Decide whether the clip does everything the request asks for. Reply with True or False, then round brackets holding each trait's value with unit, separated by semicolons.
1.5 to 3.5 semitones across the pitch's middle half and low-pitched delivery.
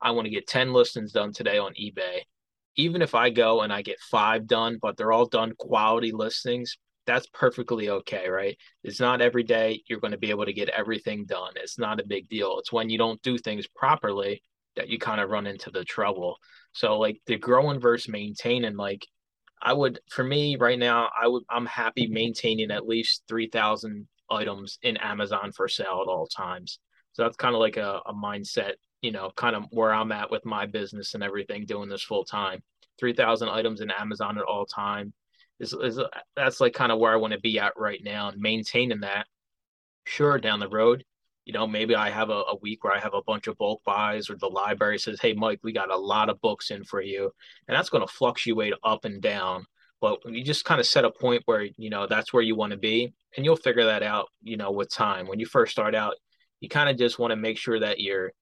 True (2.9 semitones; 115 Hz)